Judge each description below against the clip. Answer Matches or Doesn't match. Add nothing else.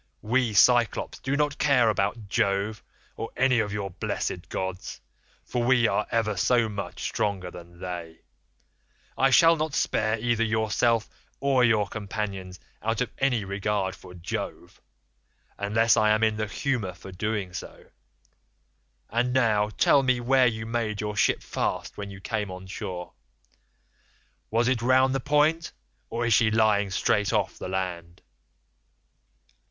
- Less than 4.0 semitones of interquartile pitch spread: Matches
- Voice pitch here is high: Doesn't match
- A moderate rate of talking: Matches